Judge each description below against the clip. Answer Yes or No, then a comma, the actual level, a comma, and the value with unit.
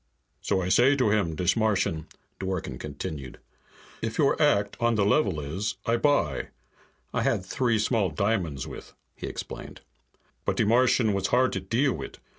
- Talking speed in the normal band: Yes, average, 165 wpm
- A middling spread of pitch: Yes, average, 4.6 semitones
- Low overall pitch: Yes, low, 105 Hz